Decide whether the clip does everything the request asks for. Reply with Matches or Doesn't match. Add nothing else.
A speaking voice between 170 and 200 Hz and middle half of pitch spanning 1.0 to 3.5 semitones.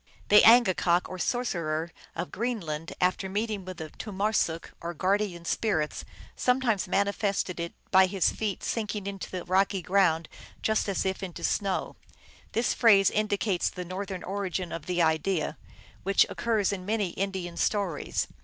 Matches